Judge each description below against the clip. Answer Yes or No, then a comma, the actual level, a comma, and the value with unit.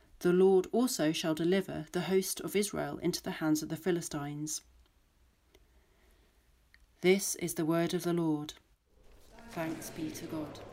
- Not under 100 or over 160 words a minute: Yes, average, 145 wpm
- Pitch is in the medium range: Yes, medium, 165 Hz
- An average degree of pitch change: Yes, average, 3.3 semitones